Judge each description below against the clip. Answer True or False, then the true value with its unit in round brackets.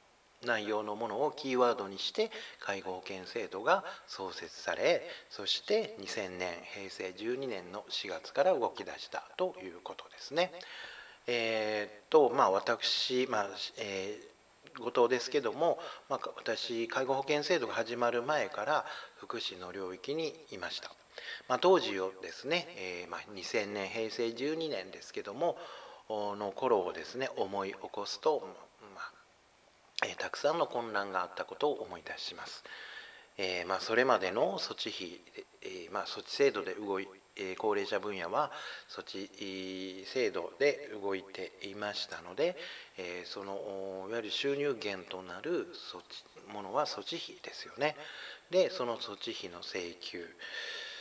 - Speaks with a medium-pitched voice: True (145 Hz)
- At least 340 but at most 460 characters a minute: False (265 characters per minute)